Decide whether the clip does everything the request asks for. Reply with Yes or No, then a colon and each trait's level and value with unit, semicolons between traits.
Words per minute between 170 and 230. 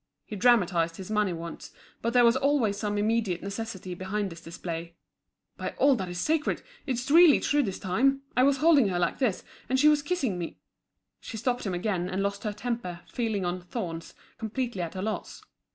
Yes: average, 190 wpm